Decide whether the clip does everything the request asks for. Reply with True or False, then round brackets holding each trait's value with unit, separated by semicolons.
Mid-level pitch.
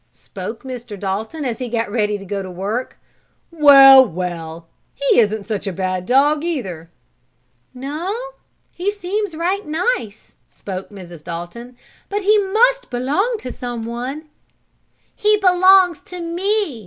False (255 Hz)